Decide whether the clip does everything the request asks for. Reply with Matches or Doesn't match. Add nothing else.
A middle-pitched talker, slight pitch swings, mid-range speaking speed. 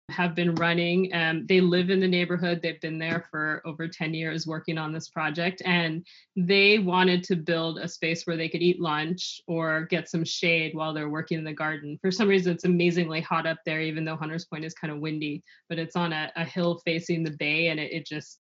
Doesn't match